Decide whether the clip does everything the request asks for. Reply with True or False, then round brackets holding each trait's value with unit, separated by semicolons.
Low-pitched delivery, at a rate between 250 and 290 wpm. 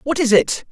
False (265 Hz; 255 wpm)